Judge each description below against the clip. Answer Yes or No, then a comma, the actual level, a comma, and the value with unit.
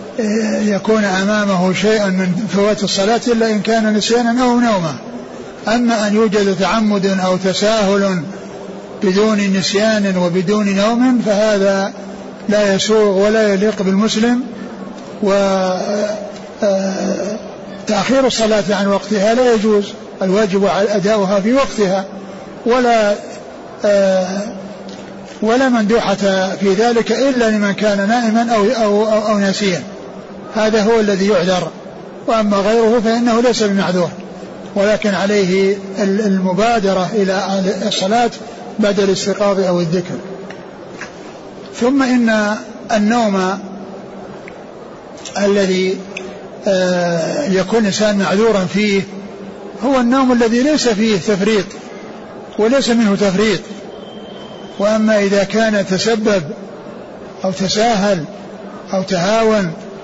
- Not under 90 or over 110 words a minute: Yes, average, 95 wpm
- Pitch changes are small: Yes, narrow, 2.0 semitones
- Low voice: No, high, 205 Hz